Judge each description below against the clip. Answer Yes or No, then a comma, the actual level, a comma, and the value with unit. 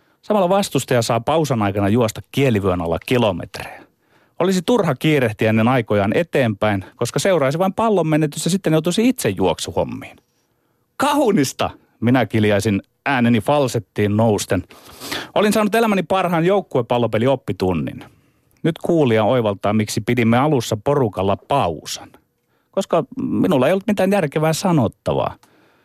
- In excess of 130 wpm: No, average, 120 wpm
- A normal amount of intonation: No, wide, 7.3 semitones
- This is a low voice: Yes, low, 130 Hz